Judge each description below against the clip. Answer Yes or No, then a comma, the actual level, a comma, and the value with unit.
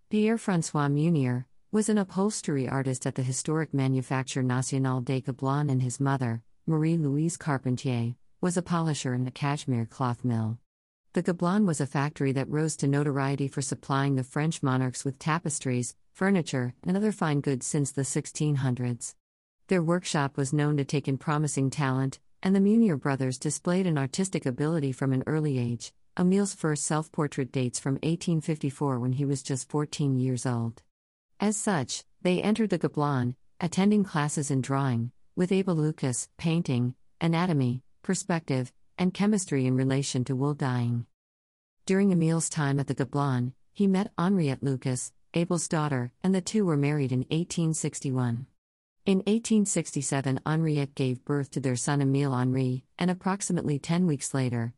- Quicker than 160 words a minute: No, average, 155 wpm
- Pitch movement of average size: Yes, average, 4.2 semitones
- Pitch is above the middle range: No, medium, 140 Hz